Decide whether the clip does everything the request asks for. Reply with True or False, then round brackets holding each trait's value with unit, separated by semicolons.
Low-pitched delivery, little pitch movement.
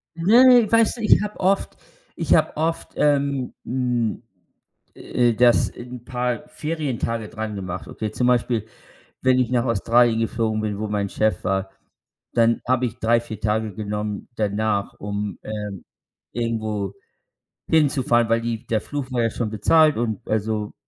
False (115 Hz; 3.1 semitones)